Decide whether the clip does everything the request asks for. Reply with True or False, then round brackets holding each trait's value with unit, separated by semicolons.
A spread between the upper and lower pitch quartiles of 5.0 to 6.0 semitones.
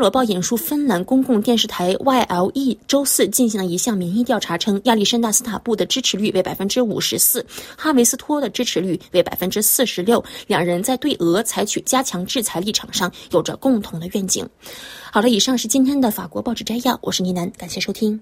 True (5.3 semitones)